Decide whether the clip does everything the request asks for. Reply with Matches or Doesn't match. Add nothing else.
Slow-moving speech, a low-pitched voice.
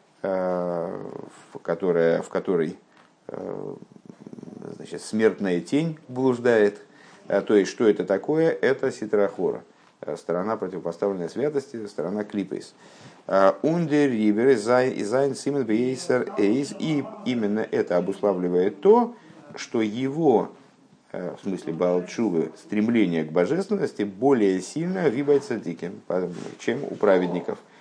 Matches